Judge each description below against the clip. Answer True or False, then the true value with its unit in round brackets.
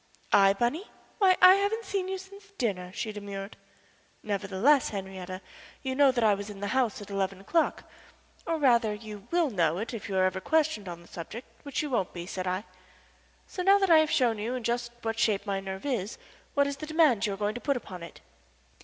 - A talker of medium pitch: False (220 Hz)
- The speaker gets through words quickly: True (225 wpm)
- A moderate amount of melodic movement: False (6.7 semitones)